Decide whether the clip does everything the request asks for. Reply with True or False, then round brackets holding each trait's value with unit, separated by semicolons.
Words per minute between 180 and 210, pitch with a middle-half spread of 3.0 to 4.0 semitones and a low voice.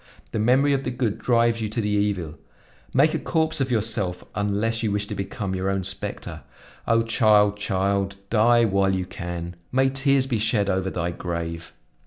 True (185 wpm; 3.5 semitones; 105 Hz)